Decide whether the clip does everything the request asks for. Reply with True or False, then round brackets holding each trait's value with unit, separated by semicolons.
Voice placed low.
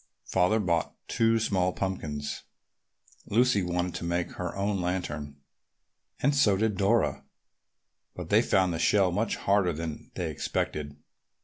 True (95 Hz)